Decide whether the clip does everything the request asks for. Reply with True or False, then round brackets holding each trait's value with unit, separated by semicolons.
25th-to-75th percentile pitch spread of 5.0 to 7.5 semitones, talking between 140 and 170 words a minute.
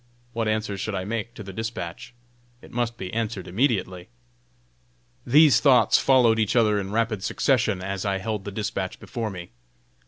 False (3.2 semitones; 165 wpm)